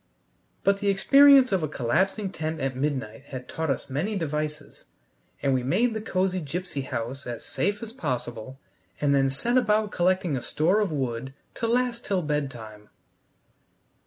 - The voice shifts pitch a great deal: Yes, wide, 7.0 semitones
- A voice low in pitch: No, medium, 155 Hz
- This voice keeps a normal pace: Yes, average, 160 wpm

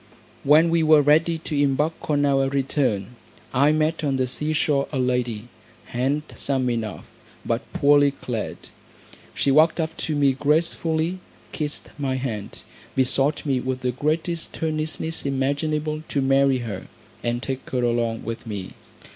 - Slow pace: No, average, 145 wpm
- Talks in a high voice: No, medium, 140 Hz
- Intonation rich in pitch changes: No, average, 3.3 semitones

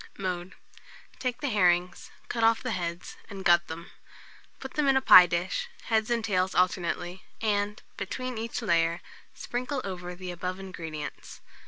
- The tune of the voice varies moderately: Yes, average, 4.5 semitones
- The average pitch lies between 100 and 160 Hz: No, high, 190 Hz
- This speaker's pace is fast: No, average, 155 wpm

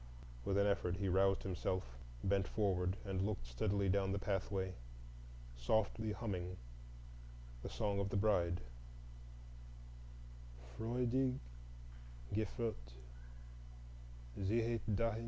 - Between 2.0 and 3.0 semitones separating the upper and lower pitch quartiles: Yes, narrow, 2.5 semitones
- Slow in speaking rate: Yes, slow, 100 wpm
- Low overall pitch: Yes, low, 100 Hz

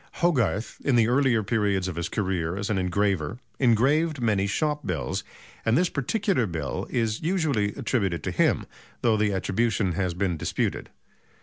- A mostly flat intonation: No, average, 5.3 semitones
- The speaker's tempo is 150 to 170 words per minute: Yes, average, 160 wpm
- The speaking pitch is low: Yes, low, 105 Hz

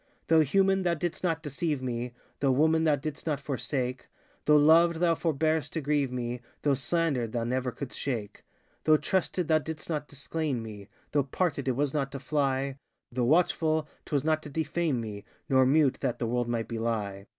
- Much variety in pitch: No, average, 4.1 semitones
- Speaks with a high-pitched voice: No, medium, 140 Hz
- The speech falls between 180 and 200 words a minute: Yes, average, 185 wpm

